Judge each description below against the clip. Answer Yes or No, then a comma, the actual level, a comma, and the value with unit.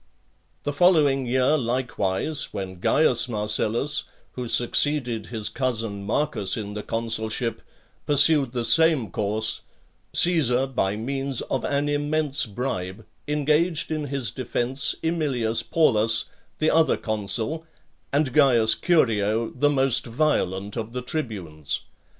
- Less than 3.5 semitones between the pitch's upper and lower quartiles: No, average, 4.9 semitones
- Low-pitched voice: Yes, low, 125 Hz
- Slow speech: Yes, slow, 120 wpm